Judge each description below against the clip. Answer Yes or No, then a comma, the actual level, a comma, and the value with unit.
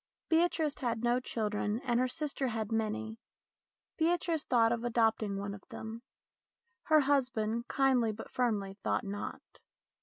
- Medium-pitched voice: No, high, 235 Hz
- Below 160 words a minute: Yes, average, 140 wpm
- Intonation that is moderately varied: Yes, average, 3.6 semitones